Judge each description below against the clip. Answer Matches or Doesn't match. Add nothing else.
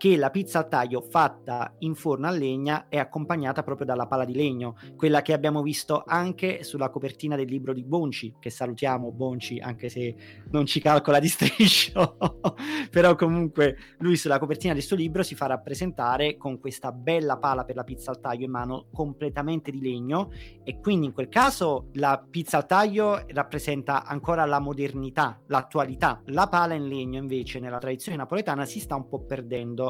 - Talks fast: Matches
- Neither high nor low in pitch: Matches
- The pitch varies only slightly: Doesn't match